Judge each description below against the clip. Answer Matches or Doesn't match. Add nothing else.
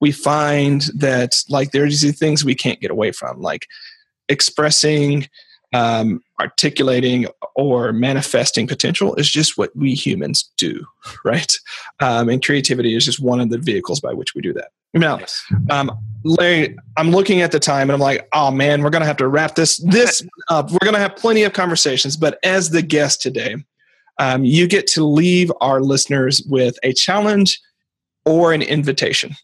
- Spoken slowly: Doesn't match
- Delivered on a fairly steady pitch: Doesn't match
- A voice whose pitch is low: Doesn't match